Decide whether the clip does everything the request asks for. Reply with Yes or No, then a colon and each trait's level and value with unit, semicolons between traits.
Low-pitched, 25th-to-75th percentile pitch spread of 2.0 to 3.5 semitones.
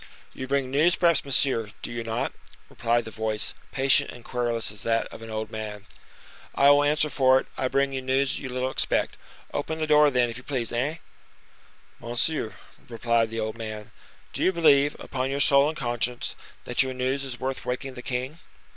Yes: low, 130 Hz; average, 3.2 semitones